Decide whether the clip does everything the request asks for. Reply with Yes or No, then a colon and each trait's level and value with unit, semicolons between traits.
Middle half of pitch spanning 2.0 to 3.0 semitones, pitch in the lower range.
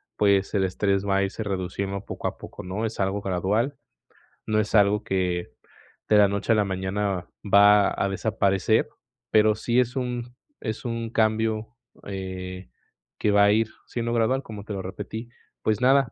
Yes: narrow, 2.4 semitones; low, 105 Hz